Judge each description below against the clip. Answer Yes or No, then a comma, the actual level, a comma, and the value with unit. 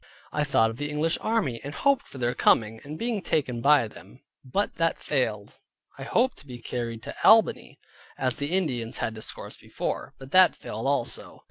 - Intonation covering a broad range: Yes, wide, 5.8 semitones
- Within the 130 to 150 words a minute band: No, average, 190 wpm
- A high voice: No, low, 135 Hz